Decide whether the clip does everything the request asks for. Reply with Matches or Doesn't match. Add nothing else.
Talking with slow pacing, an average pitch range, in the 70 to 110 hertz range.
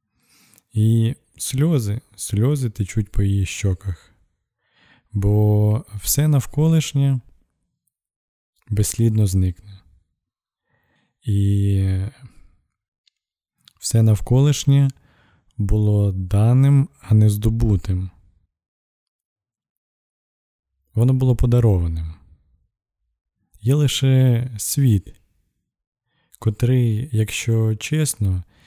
Matches